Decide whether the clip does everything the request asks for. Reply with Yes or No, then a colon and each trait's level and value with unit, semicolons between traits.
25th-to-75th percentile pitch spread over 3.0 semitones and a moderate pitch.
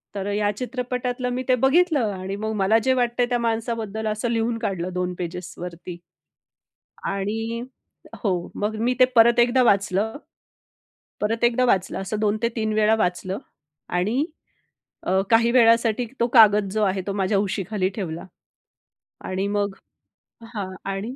No: average, 3.4 semitones; high, 215 Hz